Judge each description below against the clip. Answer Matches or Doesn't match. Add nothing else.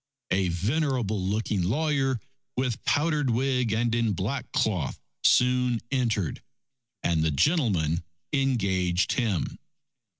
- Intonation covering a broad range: Matches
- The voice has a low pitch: Matches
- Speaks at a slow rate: Matches